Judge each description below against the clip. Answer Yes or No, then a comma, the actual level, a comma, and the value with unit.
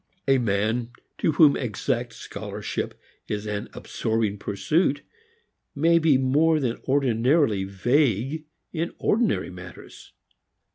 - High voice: No, low, 130 Hz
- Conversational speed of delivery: No, slow, 105 wpm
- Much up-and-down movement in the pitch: Yes, wide, 6.1 semitones